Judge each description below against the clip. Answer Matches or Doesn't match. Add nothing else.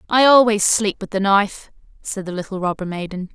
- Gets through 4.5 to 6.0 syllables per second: Matches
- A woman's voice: Matches